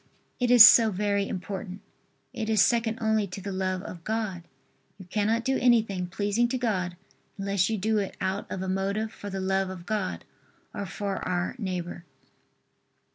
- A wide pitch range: No, average, 2.7 semitones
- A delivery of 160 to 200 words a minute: Yes, average, 175 wpm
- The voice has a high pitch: Yes, high, 200 Hz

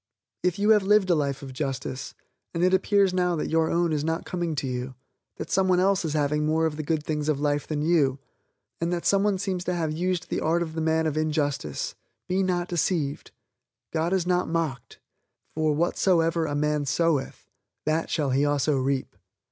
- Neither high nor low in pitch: Yes, medium, 160 Hz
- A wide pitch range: No, average, 3.3 semitones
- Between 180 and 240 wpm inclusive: Yes, average, 200 wpm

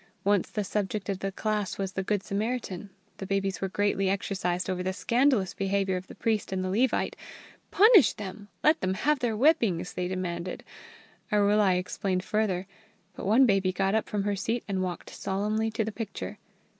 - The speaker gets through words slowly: No, average, 180 wpm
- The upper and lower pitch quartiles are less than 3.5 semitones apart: Yes, narrow, 2.4 semitones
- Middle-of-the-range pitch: No, high, 195 Hz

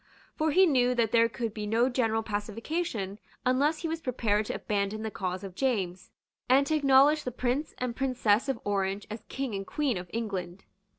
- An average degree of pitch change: Yes, average, 4.7 semitones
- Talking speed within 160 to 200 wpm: Yes, average, 190 wpm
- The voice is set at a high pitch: Yes, high, 230 Hz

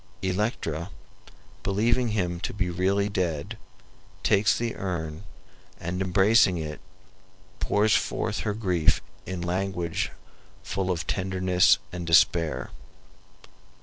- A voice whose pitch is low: Yes, very low, 95 Hz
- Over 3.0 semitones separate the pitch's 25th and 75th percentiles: No, narrow, 2.6 semitones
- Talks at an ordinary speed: No, slow, 105 wpm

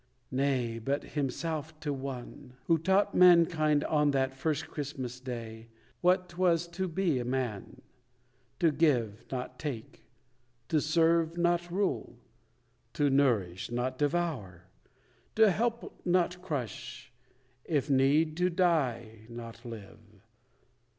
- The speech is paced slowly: Yes, slow, 115 wpm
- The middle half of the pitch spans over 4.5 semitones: Yes, wide, 5.5 semitones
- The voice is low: No, medium, 145 Hz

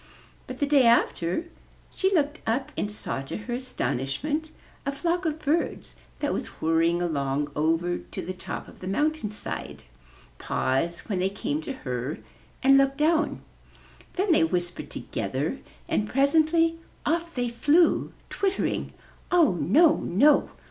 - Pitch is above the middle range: Yes, very high, 260 Hz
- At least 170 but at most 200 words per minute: No, average, 150 wpm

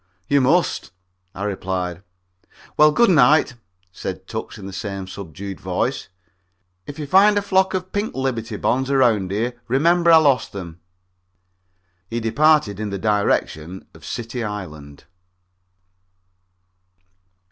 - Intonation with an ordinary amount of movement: No, wide, 7.6 semitones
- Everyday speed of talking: No, slow, 125 wpm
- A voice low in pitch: Yes, low, 115 Hz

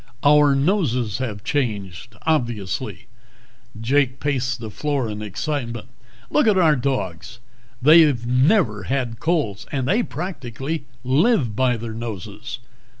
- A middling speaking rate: No, slow, 120 wpm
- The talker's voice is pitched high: No, low, 130 Hz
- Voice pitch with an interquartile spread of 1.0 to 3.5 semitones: No, average, 4.7 semitones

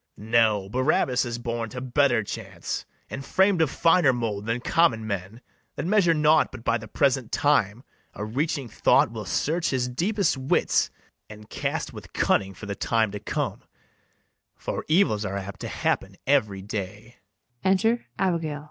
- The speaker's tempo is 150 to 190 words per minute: Yes, average, 155 wpm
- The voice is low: Yes, low, 120 Hz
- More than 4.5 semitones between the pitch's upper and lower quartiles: Yes, average, 5.3 semitones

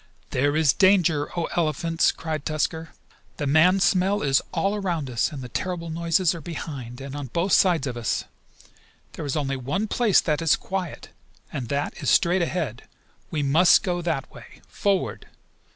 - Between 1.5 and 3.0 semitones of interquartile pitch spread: No, average, 4.2 semitones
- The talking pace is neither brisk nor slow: Yes, average, 170 wpm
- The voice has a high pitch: No, medium, 160 Hz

